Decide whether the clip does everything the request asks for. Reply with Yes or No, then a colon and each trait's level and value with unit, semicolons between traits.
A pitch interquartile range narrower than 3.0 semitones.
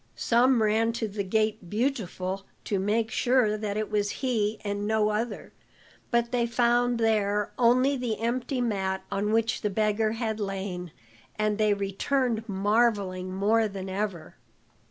Yes: narrow, 2.5 semitones